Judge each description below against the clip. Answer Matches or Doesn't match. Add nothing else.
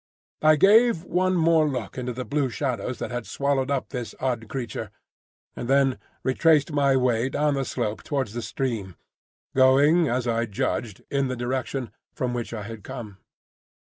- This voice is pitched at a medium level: Doesn't match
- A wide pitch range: Doesn't match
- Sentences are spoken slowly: Doesn't match